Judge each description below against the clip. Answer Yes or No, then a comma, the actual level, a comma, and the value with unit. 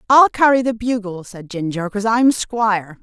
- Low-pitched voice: No, high, 215 Hz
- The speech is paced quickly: No, average, 180 wpm